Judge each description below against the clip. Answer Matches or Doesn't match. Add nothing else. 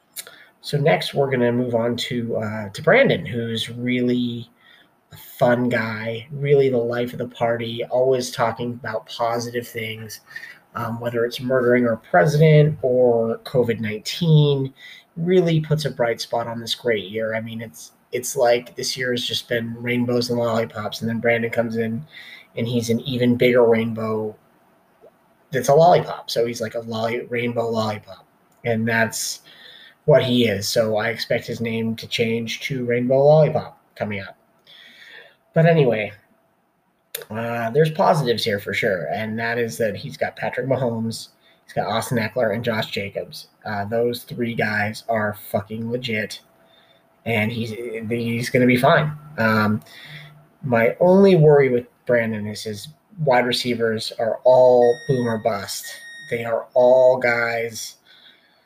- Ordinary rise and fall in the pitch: Doesn't match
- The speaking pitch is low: Matches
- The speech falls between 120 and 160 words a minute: Matches